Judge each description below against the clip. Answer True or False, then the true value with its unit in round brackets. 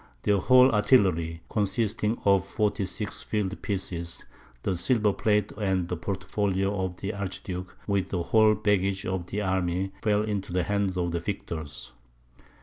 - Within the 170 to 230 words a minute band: False (145 wpm)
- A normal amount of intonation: False (2.3 semitones)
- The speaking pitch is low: True (95 Hz)